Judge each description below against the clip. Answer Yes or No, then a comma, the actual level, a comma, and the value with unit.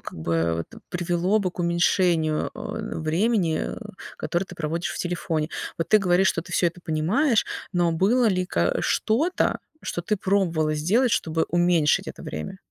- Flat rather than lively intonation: No, average, 3.2 semitones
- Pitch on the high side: No, medium, 175 Hz